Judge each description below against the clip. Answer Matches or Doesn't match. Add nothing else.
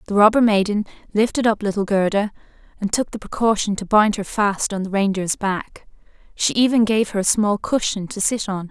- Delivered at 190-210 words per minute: Matches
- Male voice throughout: Doesn't match